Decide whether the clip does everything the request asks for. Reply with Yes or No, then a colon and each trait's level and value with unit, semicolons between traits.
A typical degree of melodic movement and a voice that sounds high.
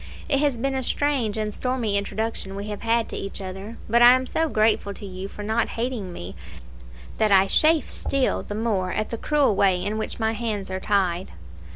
Yes: average, 3.4 semitones; high, 215 Hz